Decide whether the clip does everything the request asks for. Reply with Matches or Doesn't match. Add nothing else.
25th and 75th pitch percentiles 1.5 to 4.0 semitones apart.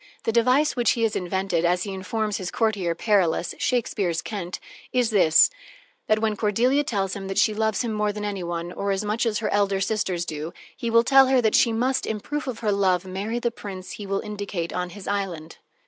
Matches